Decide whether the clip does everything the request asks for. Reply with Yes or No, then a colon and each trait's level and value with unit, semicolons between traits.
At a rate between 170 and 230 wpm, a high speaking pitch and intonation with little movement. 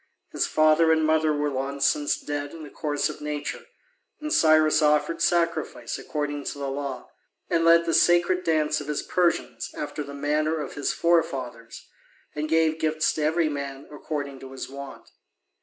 No: average, 175 wpm; medium, 150 Hz; narrow, 2.0 semitones